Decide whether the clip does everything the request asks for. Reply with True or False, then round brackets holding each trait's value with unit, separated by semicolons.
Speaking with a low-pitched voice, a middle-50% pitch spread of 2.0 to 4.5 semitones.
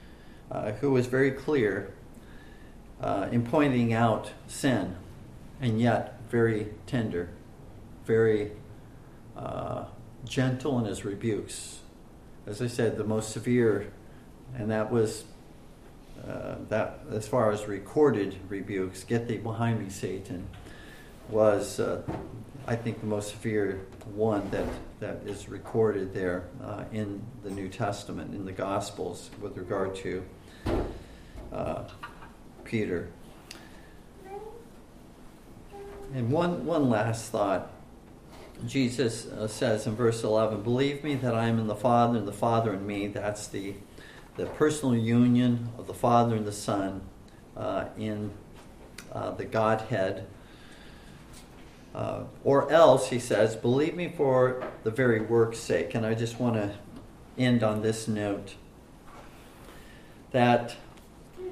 True (110 Hz; 2.9 semitones)